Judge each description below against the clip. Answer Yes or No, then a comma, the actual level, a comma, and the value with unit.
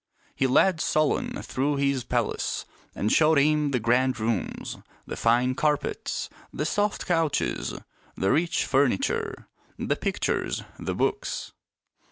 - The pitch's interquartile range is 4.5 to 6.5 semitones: No, average, 3.5 semitones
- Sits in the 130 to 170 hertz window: Yes, medium, 140 Hz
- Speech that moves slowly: Yes, slow, 125 wpm